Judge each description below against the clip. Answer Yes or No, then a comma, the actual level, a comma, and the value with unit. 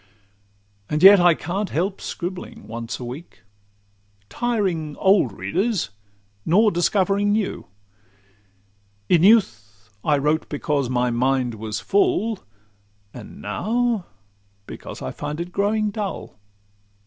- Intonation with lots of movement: Yes, wide, 8.1 semitones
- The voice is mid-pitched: Yes, medium, 175 Hz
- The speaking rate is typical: No, slow, 115 wpm